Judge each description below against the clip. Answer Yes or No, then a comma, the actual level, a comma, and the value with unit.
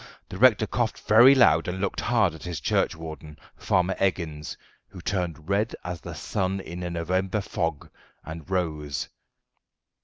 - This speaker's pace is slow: No, average, 150 wpm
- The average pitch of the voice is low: Yes, very low, 90 Hz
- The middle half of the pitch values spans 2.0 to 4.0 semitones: Yes, average, 3.3 semitones